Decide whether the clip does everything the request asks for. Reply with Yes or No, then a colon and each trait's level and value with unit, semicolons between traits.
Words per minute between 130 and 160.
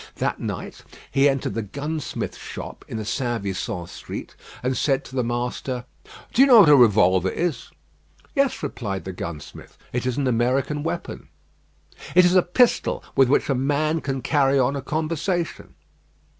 No: average, 170 wpm